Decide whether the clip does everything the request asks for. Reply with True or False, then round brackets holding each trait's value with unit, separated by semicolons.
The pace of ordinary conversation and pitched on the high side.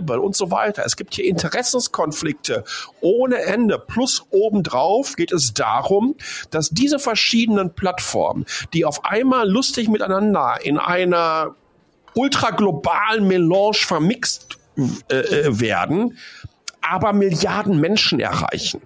False (110 wpm; 205 Hz)